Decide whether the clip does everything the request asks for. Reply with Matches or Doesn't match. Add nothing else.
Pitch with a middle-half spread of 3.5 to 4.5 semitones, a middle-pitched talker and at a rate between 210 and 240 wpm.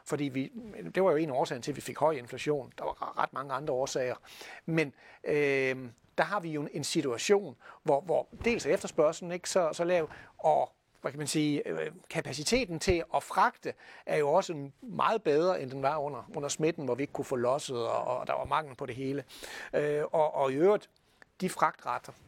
Matches